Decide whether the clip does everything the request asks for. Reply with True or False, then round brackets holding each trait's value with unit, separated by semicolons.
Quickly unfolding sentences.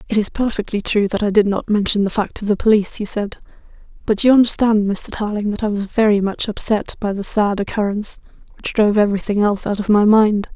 True (220 wpm)